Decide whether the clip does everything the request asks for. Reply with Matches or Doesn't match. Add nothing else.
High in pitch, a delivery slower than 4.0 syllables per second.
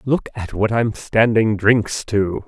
Doesn't match